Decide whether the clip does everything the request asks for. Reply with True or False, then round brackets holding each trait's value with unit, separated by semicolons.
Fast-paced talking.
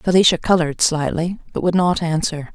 False (165 wpm)